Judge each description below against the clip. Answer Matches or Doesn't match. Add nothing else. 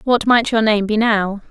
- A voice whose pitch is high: Matches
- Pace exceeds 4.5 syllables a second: Doesn't match